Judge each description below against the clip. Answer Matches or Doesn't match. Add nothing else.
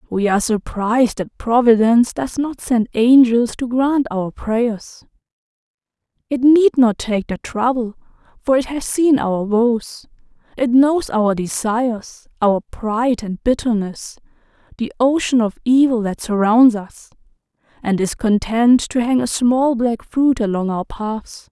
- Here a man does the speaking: Doesn't match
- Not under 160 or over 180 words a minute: Doesn't match